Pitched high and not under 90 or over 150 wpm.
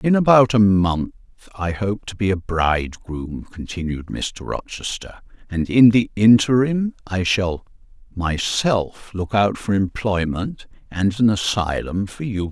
No: low, 100 Hz; average, 140 wpm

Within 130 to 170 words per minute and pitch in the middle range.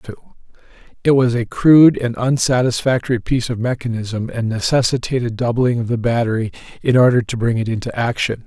No: average, 165 wpm; low, 120 Hz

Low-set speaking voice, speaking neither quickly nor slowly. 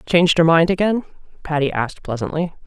No: medium, 165 Hz; average, 160 wpm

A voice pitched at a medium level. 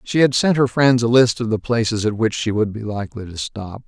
No: low, 115 Hz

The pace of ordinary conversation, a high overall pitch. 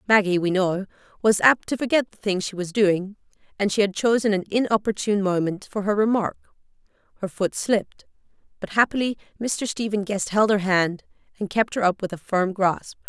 Yes: average, 190 wpm; high, 200 Hz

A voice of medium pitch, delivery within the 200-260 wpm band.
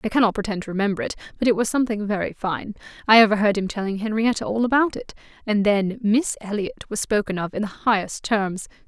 No: high, 215 Hz; fast, 205 wpm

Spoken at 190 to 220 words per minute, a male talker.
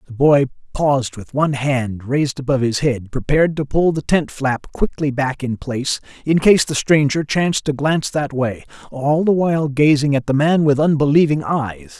Yes: average, 195 wpm; male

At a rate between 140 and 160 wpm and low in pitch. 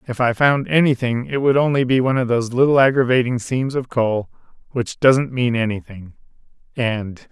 No: average, 170 wpm; low, 125 Hz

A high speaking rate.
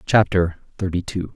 No: slow, 135 wpm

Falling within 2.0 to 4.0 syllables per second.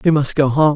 No: 5.7 syllables/s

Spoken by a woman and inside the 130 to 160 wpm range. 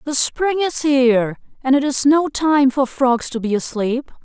No: female; average, 200 wpm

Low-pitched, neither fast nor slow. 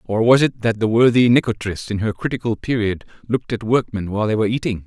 No: low, 110 Hz; fast, 220 wpm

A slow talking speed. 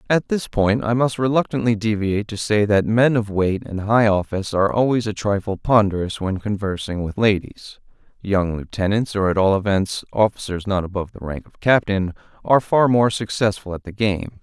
No: average, 180 wpm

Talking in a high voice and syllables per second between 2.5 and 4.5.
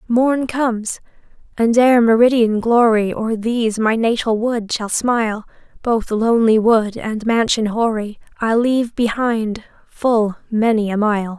Yes: high, 225 Hz; 4.2 syllables/s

